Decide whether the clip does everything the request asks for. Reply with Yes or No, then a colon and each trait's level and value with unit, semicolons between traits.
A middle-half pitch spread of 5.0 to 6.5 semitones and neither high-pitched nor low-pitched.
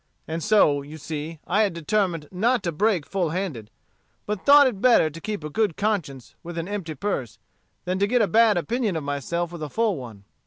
Yes: wide, 5.4 semitones; medium, 175 Hz